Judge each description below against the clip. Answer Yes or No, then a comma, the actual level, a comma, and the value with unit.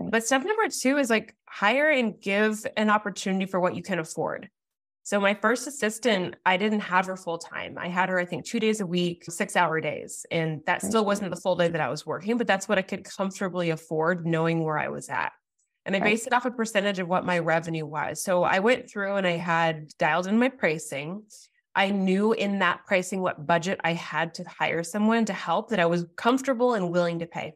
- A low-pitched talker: No, high, 190 Hz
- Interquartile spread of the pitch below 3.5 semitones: No, average, 4.1 semitones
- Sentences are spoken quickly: Yes, fast, 230 wpm